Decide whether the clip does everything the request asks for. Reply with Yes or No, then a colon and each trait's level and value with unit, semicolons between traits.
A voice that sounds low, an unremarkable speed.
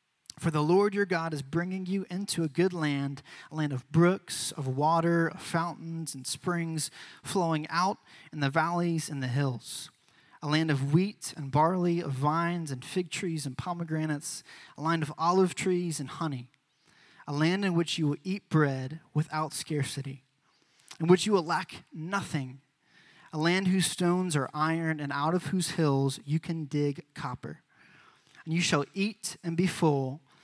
No: medium, 160 Hz; average, 175 wpm